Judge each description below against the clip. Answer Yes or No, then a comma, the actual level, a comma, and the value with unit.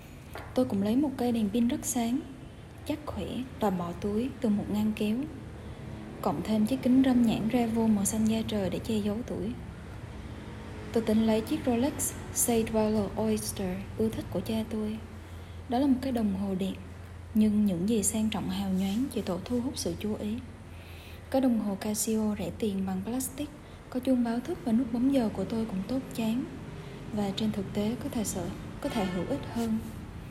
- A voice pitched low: No, high, 215 Hz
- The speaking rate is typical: Yes, average, 200 wpm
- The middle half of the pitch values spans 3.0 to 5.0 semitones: No, wide, 5.4 semitones